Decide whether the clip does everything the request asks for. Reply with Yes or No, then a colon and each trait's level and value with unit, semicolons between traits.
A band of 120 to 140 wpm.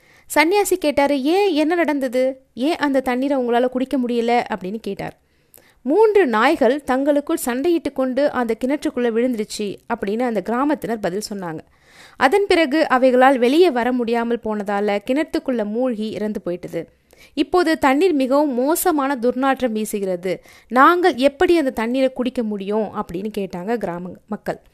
Yes: fast, 130 wpm